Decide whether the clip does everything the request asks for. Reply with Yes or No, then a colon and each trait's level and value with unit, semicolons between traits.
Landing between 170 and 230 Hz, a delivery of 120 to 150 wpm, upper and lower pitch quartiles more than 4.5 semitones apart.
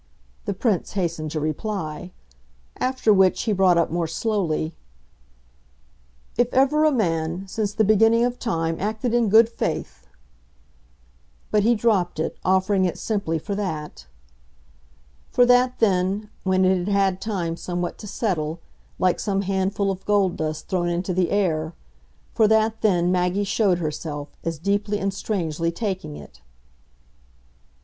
No: high, 190 Hz; average, 145 wpm; average, 4.0 semitones